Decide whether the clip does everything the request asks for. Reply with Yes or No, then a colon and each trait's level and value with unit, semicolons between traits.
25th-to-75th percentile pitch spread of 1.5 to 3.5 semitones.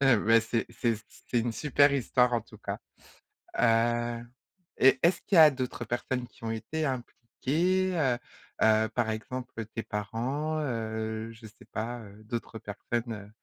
Yes: average, 2.8 semitones